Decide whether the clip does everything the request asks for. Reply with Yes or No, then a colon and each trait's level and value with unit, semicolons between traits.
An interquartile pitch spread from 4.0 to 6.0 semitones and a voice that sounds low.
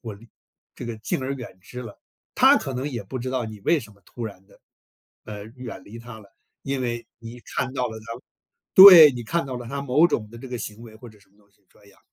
No: average, 3.1 semitones; low, 120 Hz